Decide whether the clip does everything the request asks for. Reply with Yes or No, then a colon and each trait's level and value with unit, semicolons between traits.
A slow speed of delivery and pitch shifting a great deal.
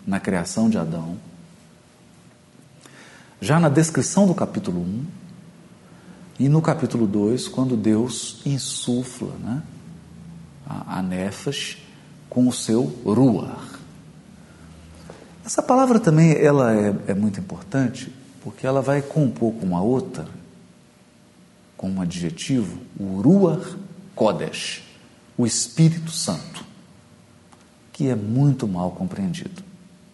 Yes: slow, 105 wpm; wide, 7.7 semitones